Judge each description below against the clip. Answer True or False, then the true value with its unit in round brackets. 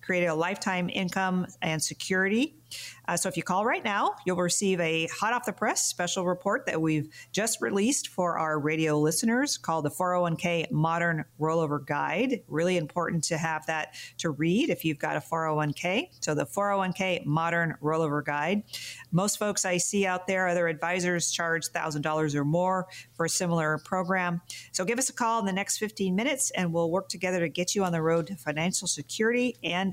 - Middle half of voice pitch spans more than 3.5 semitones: False (3.0 semitones)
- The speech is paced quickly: False (190 wpm)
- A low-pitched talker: False (175 Hz)